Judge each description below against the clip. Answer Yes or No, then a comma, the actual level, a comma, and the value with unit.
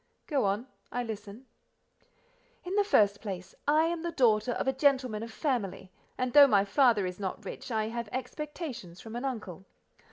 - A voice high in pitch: Yes, high, 235 Hz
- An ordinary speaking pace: Yes, average, 180 wpm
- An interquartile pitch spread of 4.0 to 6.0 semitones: Yes, average, 5.1 semitones